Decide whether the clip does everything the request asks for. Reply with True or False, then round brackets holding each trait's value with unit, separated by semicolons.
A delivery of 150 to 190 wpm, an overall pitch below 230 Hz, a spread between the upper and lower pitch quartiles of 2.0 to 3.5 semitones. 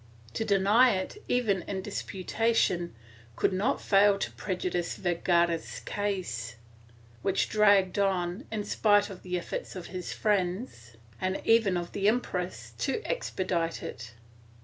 False (135 wpm; 190 Hz; 2.8 semitones)